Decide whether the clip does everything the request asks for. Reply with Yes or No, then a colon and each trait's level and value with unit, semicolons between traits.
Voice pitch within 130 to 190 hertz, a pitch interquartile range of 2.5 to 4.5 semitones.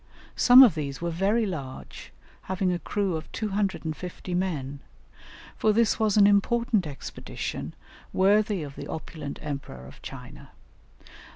No: medium, 185 Hz; average, 5.1 semitones